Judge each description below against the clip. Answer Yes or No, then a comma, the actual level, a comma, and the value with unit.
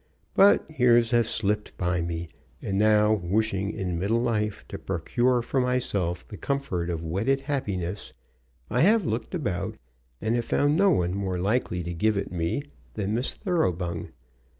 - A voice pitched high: No, low, 105 Hz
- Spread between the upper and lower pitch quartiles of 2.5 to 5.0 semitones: No, wide, 5.5 semitones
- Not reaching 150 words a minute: No, average, 160 wpm